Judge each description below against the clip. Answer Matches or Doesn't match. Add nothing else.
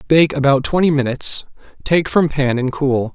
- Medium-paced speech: Matches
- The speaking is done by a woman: Doesn't match